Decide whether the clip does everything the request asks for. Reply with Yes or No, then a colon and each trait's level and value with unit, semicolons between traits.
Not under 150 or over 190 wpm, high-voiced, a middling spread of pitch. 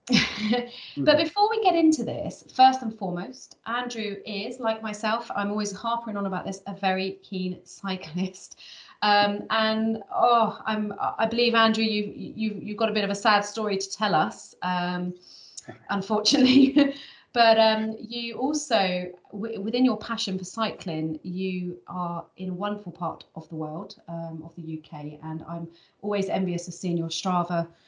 Yes: average, 165 wpm; high, 205 Hz; average, 3.8 semitones